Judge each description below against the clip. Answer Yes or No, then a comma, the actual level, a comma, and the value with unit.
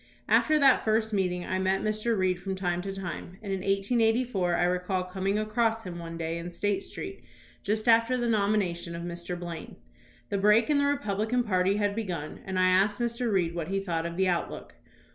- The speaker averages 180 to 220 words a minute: Yes, average, 200 wpm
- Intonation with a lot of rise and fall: No, average, 3.6 semitones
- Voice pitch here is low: No, high, 195 Hz